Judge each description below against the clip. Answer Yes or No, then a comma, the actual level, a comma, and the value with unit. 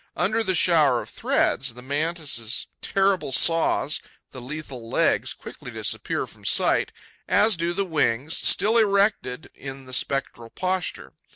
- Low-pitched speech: No, medium, 155 Hz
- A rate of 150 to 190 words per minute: No, slow, 135 wpm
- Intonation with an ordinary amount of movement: No, wide, 6.1 semitones